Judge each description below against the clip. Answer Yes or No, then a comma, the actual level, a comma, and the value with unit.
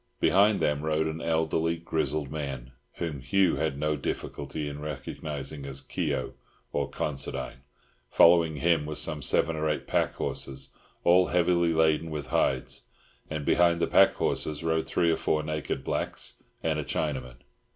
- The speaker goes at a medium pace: Yes, average, 150 wpm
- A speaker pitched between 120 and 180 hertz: No, very low, 75 Hz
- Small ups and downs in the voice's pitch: Yes, narrow, 2.3 semitones